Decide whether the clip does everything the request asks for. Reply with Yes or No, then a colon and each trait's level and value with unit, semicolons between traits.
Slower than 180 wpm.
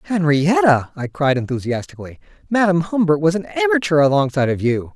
Yes: average, 145 wpm